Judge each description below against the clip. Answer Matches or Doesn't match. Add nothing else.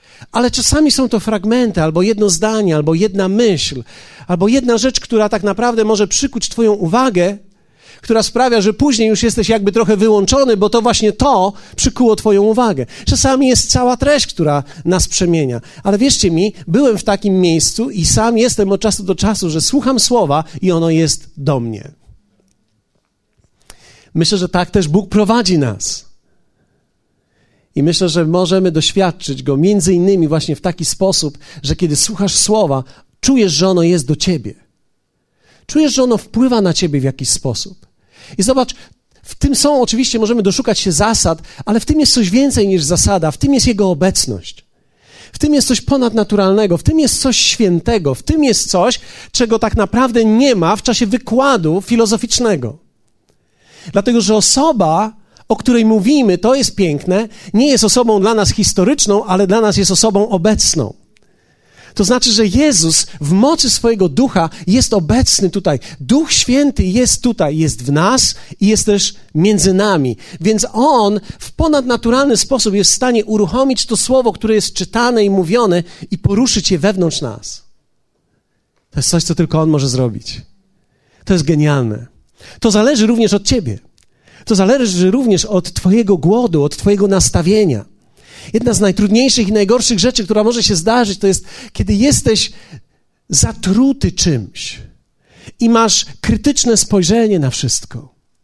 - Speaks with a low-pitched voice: Doesn't match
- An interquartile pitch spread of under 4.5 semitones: Doesn't match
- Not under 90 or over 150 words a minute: Doesn't match